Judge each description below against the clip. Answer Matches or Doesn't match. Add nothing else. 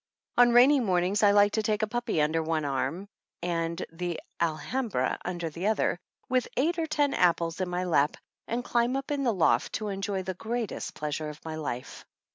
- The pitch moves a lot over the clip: Matches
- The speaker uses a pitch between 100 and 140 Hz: Doesn't match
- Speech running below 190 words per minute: Doesn't match